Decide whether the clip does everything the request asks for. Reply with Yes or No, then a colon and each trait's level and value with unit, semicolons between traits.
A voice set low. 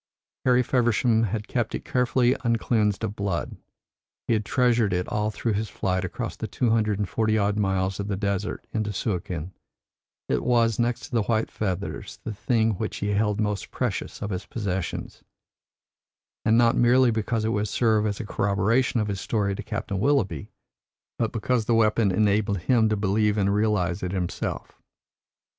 Yes: low, 105 Hz